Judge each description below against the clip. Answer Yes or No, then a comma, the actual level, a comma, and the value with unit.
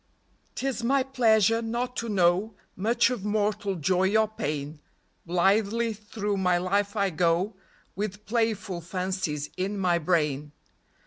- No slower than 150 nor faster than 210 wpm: No, slow, 135 wpm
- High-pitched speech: Yes, high, 200 Hz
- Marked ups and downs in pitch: No, average, 3.5 semitones